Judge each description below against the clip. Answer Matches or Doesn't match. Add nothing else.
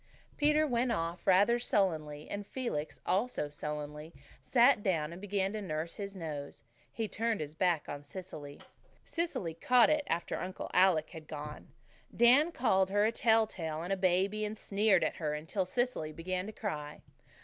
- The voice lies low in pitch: Doesn't match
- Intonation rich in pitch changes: Matches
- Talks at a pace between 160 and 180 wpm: Matches